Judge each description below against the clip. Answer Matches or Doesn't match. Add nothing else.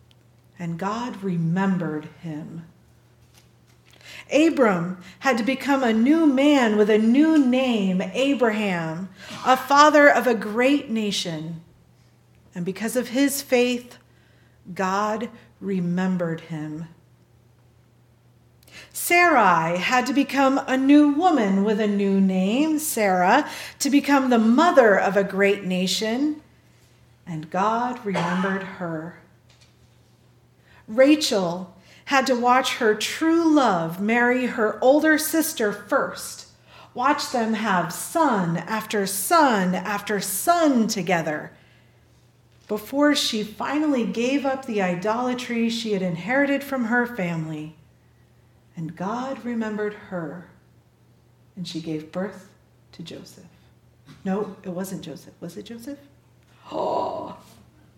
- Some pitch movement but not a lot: Doesn't match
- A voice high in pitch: Matches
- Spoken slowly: Matches